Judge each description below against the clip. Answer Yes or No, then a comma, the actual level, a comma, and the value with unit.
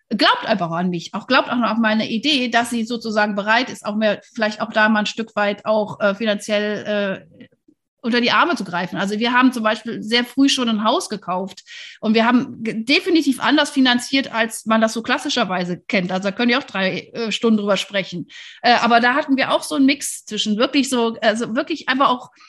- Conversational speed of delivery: No, fast, 225 wpm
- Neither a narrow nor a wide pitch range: Yes, average, 3.8 semitones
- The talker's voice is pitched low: No, high, 230 Hz